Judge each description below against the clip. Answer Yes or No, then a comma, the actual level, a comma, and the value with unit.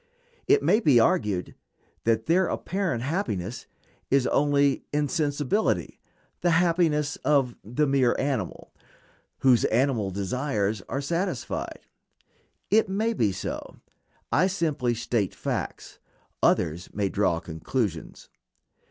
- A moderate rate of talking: No, slow, 110 wpm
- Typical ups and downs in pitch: No, wide, 6.7 semitones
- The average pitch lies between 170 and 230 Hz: No, low, 135 Hz